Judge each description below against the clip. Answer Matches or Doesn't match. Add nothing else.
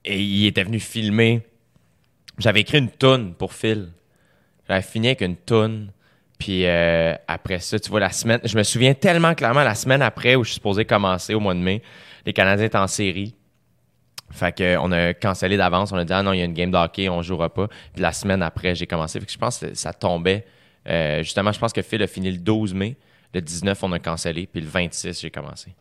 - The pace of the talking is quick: Matches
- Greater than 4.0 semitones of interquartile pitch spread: Doesn't match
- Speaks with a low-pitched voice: Matches